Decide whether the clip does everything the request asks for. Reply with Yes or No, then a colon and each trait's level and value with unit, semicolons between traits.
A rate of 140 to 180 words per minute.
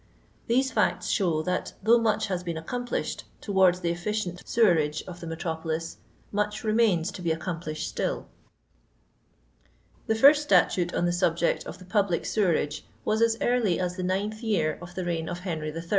Yes: average, 170 wpm